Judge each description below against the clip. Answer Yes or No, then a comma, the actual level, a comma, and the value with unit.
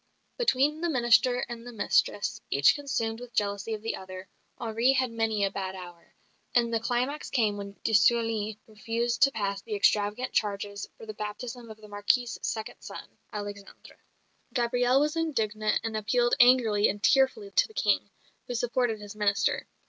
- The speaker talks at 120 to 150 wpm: No, average, 170 wpm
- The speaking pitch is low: No, high, 225 Hz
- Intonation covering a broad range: No, average, 3.0 semitones